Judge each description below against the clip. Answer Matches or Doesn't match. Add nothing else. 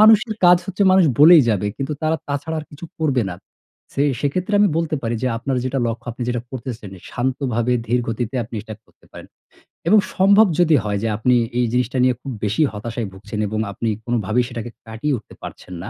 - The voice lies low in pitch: Matches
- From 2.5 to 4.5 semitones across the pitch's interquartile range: Doesn't match